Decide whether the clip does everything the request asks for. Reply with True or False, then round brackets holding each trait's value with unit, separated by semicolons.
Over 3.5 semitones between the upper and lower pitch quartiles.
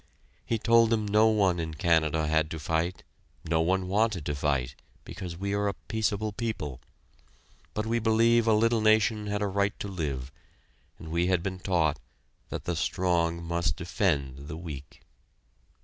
True (4.9 semitones)